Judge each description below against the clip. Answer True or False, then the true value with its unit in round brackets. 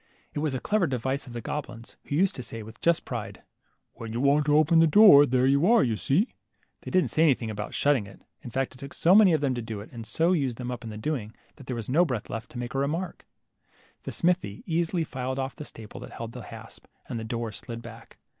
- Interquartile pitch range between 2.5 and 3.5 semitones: False (5.2 semitones)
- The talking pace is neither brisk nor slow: False (260 wpm)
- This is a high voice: False (130 Hz)